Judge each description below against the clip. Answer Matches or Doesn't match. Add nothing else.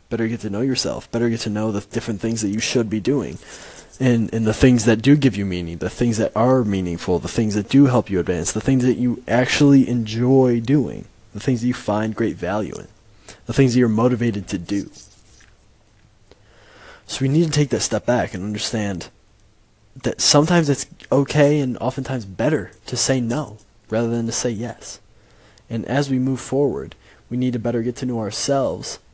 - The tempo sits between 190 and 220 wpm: Matches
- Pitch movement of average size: Matches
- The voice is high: Doesn't match